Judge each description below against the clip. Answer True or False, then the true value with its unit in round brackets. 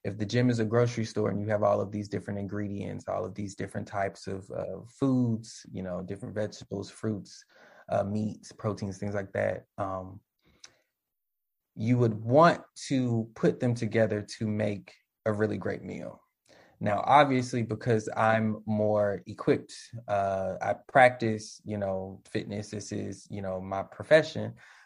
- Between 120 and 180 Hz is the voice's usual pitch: False (105 Hz)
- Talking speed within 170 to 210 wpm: False (160 wpm)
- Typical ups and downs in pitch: False (2.1 semitones)